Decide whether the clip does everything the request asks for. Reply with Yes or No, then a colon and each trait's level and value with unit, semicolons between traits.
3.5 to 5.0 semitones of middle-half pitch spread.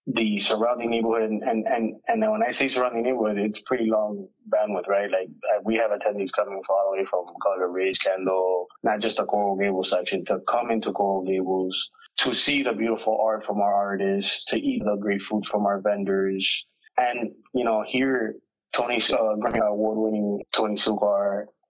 No: narrow, 2.4 semitones